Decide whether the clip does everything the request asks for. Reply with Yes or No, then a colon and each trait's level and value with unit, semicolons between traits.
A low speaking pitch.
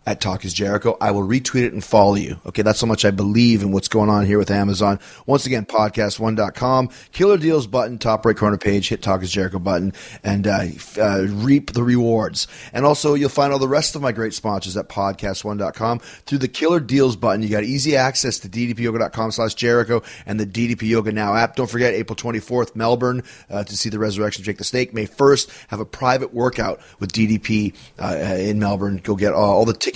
Yes: low, 110 Hz